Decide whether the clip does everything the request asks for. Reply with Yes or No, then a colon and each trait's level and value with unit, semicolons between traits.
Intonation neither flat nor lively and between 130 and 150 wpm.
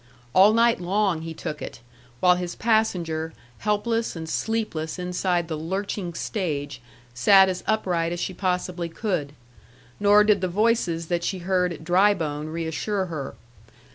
Yes: average, 3.8 semitones; average, 145 wpm